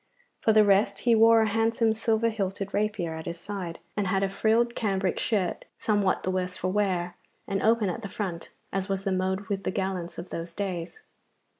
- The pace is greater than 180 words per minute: Yes, average, 200 wpm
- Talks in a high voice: Yes, high, 195 Hz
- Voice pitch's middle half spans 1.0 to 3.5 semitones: Yes, average, 2.8 semitones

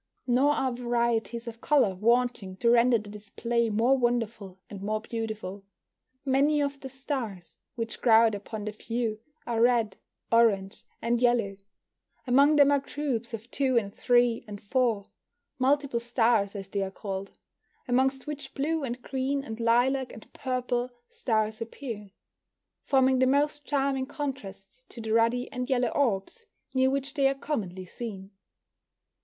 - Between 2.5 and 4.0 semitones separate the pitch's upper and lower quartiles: Yes, average, 3.5 semitones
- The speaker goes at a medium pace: Yes, average, 150 wpm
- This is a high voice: Yes, high, 240 Hz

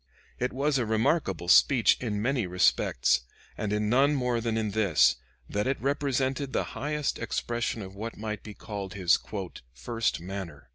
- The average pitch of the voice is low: Yes, low, 110 Hz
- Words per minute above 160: Yes, average, 170 wpm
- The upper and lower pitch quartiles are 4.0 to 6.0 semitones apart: Yes, average, 4.9 semitones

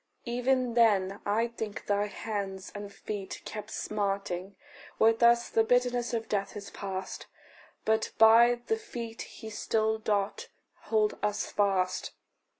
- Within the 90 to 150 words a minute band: Yes, slow, 135 wpm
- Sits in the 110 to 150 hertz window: No, high, 215 Hz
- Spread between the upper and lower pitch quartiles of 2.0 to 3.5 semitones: Yes, narrow, 2.6 semitones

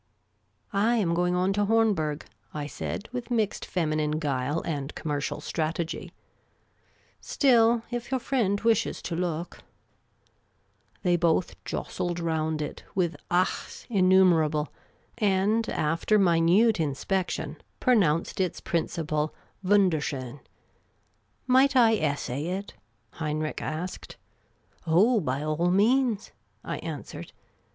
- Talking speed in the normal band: No, slow, 125 wpm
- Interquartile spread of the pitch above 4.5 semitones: Yes, average, 5.1 semitones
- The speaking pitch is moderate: Yes, medium, 175 Hz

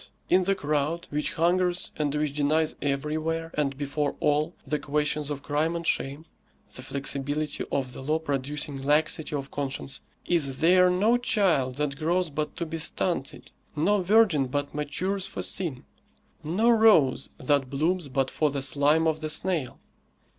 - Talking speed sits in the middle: Yes, average, 160 wpm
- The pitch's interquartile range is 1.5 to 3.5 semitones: Yes, average, 3.2 semitones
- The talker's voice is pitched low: No, medium, 150 Hz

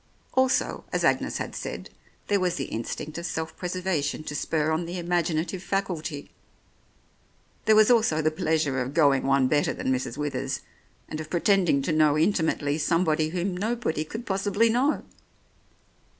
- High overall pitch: No, medium, 160 Hz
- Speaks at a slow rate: No, average, 160 wpm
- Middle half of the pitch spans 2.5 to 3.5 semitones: No, average, 4.2 semitones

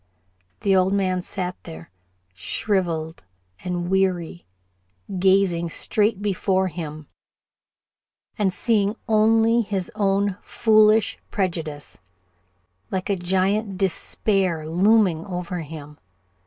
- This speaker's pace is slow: Yes, slow, 95 wpm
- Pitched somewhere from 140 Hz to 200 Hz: Yes, high, 190 Hz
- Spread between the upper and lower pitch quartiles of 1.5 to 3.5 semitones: Yes, average, 3.0 semitones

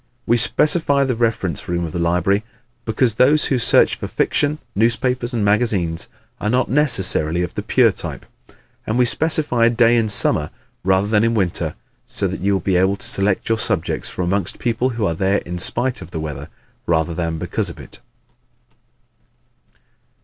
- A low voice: Yes, low, 105 Hz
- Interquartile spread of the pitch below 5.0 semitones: No, wide, 5.4 semitones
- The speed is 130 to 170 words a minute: No, average, 180 wpm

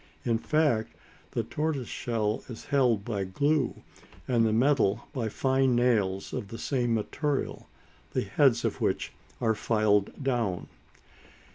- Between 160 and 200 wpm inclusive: No, slow, 135 wpm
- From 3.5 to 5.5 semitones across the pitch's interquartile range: Yes, average, 3.8 semitones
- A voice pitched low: Yes, low, 115 Hz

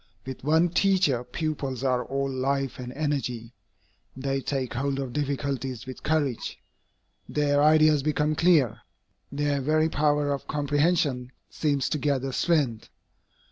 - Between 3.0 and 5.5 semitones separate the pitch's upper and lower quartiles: No, narrow, 2.4 semitones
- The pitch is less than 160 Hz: Yes, medium, 140 Hz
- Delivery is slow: Yes, slow, 130 wpm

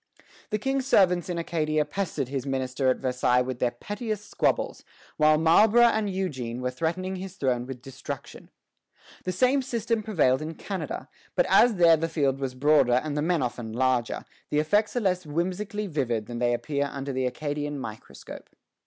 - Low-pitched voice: No, medium, 155 Hz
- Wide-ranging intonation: Yes, wide, 6.7 semitones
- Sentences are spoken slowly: No, average, 175 wpm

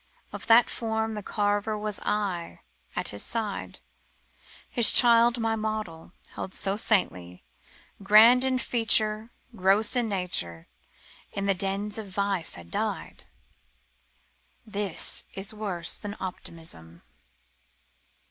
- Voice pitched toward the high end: Yes, high, 205 Hz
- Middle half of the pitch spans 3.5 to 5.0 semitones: No, average, 3.0 semitones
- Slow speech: Yes, slow, 115 wpm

